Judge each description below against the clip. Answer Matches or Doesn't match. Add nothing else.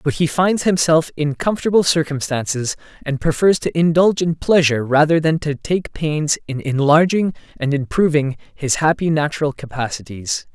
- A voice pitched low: Doesn't match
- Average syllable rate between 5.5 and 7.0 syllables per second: Doesn't match